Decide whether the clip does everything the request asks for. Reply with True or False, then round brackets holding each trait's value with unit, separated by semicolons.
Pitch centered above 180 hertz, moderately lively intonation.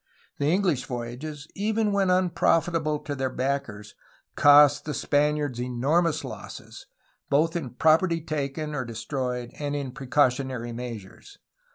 False (145 Hz; 4.1 semitones)